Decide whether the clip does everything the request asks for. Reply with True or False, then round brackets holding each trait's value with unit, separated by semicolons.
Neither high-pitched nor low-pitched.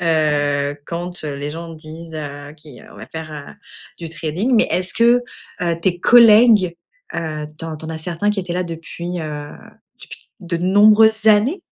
True (170 Hz)